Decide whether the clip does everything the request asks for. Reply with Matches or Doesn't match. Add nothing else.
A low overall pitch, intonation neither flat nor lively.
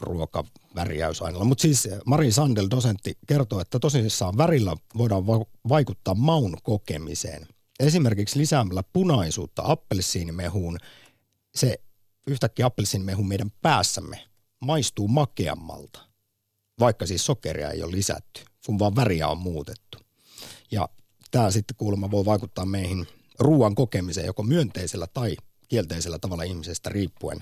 Matches